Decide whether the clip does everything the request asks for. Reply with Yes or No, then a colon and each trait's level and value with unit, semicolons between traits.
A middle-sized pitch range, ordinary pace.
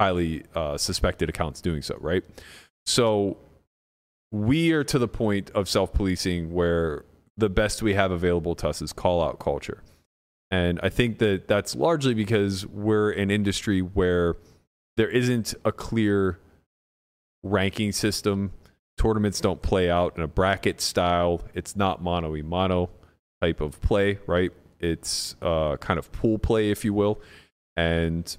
Yes: average, 4.0 semitones; average, 145 wpm